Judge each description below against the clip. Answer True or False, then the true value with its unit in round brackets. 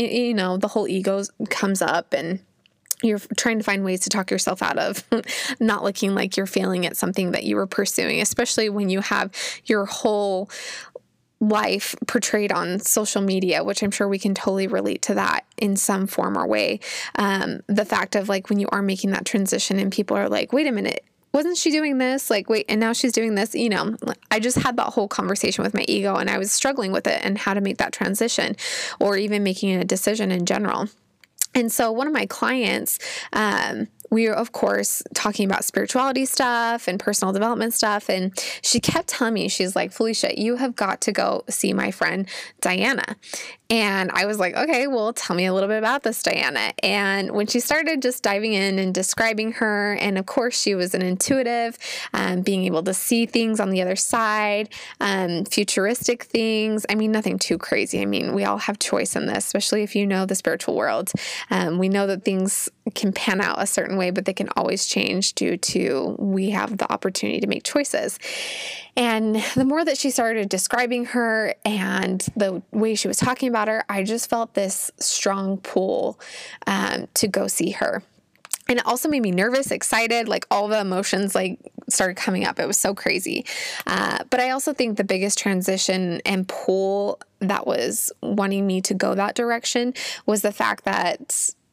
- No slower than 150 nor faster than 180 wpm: False (200 wpm)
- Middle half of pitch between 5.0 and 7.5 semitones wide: False (3.2 semitones)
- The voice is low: False (210 Hz)